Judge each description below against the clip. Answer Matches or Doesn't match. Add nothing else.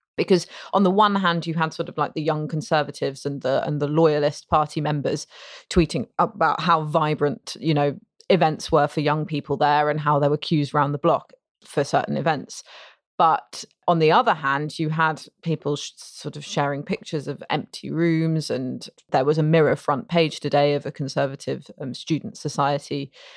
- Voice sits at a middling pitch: Matches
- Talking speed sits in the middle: Matches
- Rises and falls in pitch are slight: Matches